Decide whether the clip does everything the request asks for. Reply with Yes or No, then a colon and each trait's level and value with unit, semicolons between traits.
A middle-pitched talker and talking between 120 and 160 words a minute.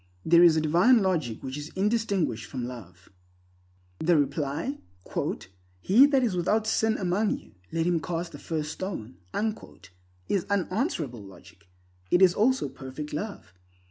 Yes: medium, 170 Hz; average, 140 wpm